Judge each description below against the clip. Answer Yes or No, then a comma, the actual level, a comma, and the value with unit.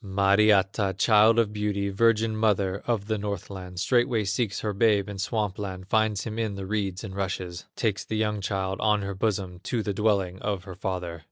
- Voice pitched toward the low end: Yes, low, 100 Hz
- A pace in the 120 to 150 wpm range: No, average, 190 wpm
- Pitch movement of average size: No, narrow, 2.1 semitones